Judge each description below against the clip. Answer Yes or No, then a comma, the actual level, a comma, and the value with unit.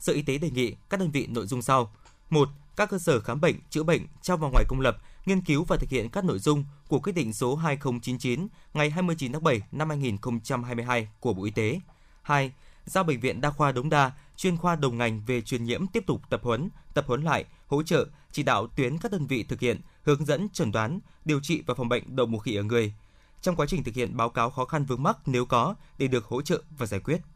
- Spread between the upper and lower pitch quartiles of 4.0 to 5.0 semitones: Yes, average, 4.7 semitones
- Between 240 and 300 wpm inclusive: Yes, fast, 250 wpm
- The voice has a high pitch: No, medium, 140 Hz